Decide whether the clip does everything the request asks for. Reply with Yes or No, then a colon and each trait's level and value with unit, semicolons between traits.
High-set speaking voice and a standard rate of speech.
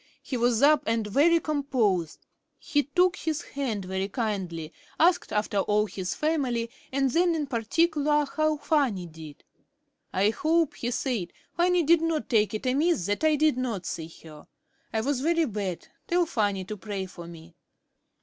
Yes: high, 245 Hz; average, 165 wpm